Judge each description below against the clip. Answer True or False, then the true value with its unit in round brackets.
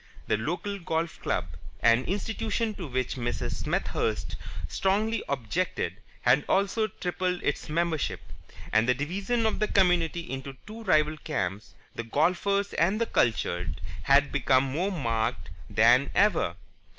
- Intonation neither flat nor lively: False (7.6 semitones)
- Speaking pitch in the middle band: True (160 Hz)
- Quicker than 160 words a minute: False (135 wpm)